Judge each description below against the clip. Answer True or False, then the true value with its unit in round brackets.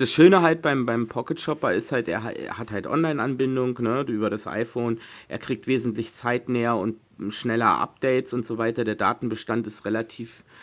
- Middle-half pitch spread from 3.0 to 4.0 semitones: False (2.6 semitones)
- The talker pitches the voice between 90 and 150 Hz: True (115 Hz)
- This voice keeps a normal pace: True (170 wpm)